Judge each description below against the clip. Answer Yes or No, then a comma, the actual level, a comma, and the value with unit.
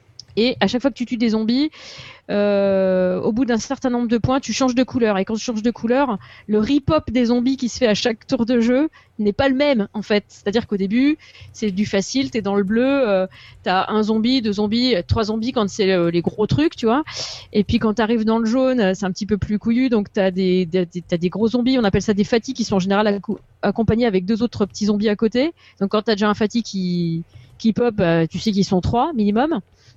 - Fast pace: Yes, fast, 260 wpm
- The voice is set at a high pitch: Yes, high, 220 Hz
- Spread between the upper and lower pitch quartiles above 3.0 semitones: Yes, average, 3.4 semitones